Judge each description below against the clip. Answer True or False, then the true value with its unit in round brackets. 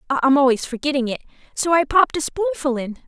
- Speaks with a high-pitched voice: True (285 Hz)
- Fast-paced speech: False (195 wpm)